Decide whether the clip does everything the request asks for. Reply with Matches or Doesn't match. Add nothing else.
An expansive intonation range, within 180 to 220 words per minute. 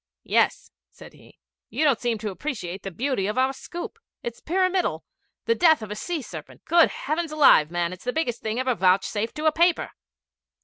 Matches